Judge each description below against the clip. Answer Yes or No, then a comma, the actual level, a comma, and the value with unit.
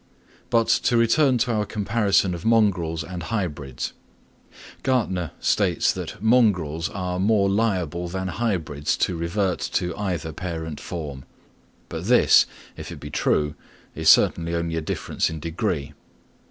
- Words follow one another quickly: No, average, 140 wpm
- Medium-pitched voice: No, very low, 90 Hz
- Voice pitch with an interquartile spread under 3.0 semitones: No, average, 4.7 semitones